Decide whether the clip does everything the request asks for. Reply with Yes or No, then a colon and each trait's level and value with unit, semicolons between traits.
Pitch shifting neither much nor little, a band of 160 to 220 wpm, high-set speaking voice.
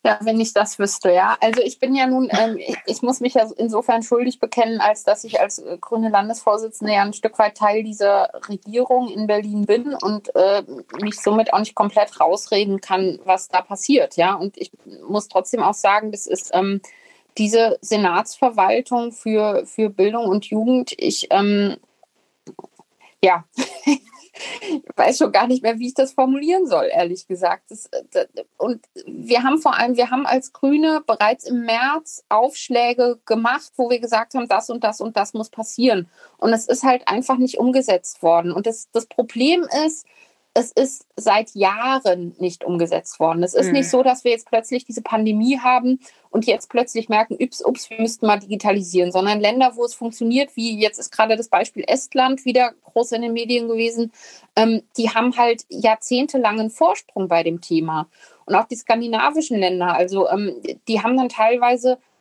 Yes: average, 3.6 semitones; average, 175 wpm; high, 225 Hz